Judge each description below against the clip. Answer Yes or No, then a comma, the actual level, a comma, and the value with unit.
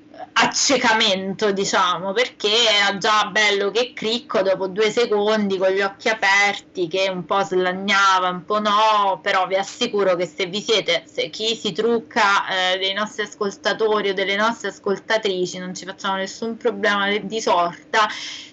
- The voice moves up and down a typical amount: No, narrow, 2.3 semitones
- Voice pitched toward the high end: Yes, high, 205 Hz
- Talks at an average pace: Yes, average, 155 wpm